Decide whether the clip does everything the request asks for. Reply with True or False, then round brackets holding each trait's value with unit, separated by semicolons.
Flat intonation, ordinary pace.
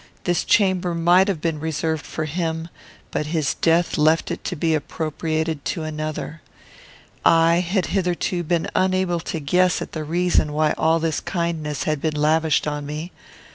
True (2.2 semitones; 165 wpm)